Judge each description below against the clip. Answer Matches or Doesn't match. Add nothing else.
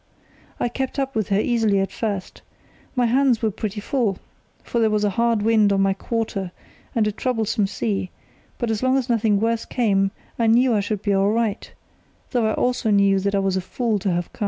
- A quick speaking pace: Matches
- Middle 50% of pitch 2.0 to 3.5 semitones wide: Matches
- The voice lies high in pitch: Matches